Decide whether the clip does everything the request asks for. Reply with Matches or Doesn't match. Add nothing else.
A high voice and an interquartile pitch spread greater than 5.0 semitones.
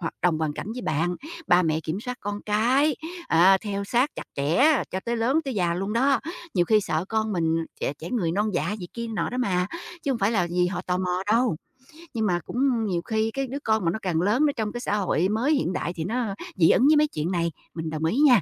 Matches